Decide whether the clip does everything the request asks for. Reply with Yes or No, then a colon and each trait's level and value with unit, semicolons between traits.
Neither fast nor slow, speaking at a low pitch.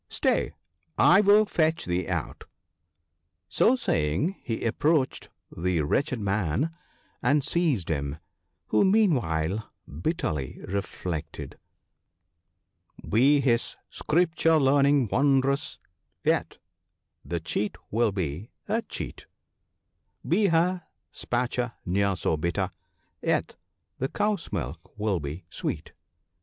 No: slow, 110 wpm; low, 115 Hz